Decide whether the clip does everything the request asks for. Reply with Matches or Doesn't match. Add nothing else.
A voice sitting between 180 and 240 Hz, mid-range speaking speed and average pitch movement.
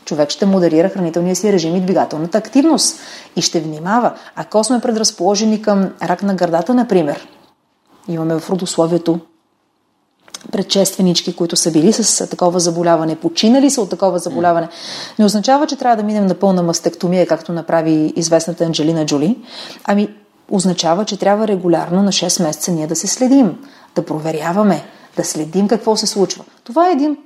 Matches